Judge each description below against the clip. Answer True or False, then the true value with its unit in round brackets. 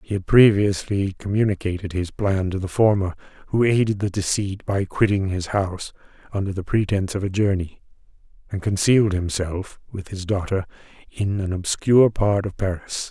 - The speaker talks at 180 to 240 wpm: False (160 wpm)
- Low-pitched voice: True (100 Hz)